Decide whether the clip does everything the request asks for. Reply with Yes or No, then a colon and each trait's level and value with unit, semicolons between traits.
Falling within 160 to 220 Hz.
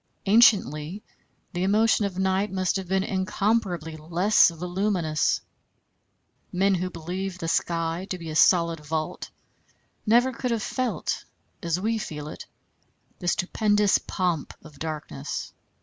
Yes: medium, 185 Hz